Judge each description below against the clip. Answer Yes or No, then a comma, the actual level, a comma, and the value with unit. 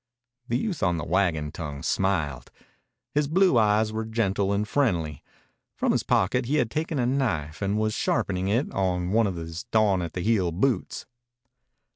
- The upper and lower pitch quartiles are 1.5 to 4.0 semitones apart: No, average, 4.9 semitones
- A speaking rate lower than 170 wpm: No, average, 175 wpm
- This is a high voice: No, low, 100 Hz